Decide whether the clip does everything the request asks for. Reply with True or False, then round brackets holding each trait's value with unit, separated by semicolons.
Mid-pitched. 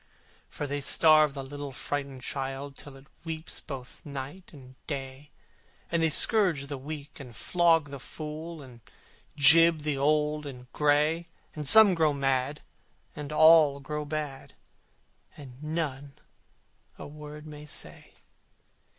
True (145 Hz)